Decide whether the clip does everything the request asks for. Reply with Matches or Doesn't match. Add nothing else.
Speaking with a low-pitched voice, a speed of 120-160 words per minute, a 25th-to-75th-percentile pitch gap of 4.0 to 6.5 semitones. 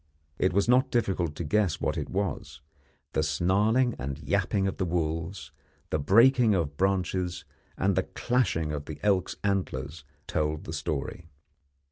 Matches